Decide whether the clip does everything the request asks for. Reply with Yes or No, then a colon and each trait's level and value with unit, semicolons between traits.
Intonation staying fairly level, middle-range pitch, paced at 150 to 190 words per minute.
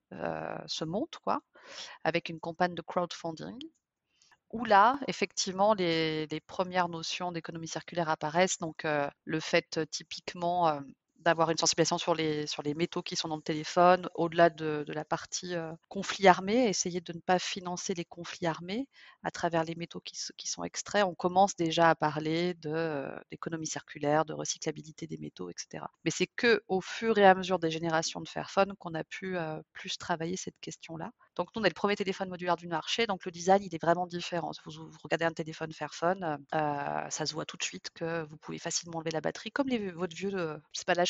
No: narrow, 2.3 semitones; medium, 170 Hz; average, 205 wpm